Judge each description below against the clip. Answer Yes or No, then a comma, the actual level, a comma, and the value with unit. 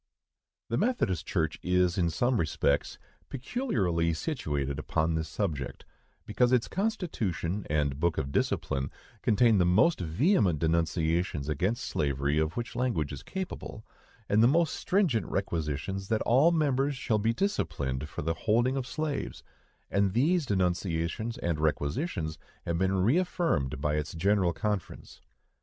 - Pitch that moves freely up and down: Yes, wide, 7.9 semitones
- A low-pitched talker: Yes, very low, 95 Hz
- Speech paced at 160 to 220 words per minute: No, average, 140 wpm